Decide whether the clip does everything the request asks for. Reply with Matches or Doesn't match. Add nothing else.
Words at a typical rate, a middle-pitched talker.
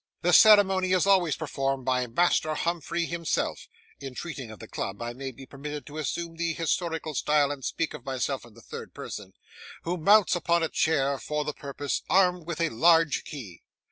Matches